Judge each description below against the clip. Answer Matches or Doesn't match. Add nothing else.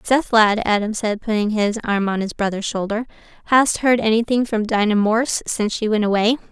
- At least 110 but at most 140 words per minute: Doesn't match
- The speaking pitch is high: Matches